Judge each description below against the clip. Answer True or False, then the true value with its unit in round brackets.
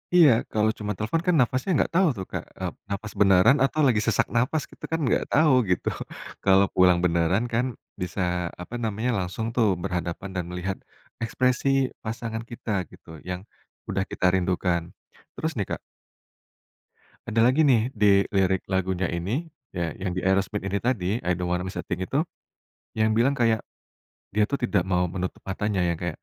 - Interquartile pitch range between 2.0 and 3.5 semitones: False (4.5 semitones)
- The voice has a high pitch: False (100 Hz)